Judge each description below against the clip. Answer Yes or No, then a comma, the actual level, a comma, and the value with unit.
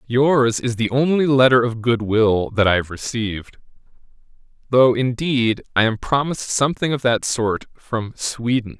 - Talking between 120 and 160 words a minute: Yes, average, 150 wpm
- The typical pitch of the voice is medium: No, low, 120 Hz